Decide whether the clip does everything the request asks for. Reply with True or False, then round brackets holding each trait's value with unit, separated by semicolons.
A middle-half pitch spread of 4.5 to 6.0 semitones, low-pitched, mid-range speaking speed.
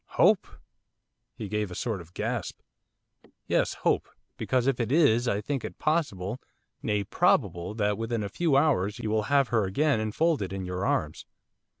True (5.4 semitones; 110 Hz; 170 wpm)